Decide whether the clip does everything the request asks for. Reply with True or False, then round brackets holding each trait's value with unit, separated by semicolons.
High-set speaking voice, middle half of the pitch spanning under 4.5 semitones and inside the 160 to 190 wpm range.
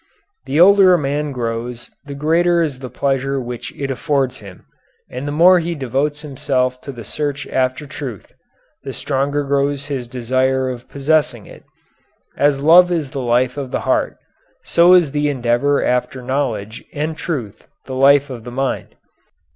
False (135 Hz; 2.6 semitones; 165 wpm)